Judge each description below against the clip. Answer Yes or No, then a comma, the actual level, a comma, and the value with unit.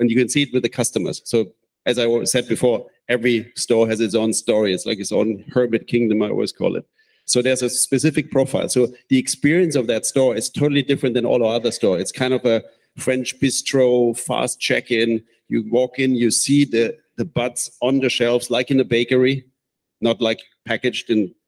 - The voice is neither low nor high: No, low, 125 Hz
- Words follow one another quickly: Yes, fast, 210 wpm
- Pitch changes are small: Yes, narrow, 2.1 semitones